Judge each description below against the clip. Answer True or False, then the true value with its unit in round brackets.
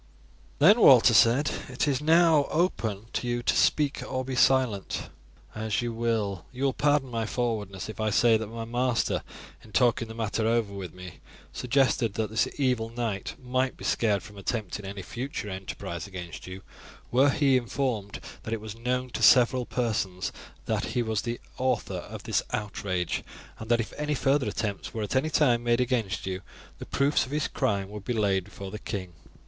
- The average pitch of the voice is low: True (115 Hz)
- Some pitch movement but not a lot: True (3.9 semitones)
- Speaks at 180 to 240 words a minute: True (185 wpm)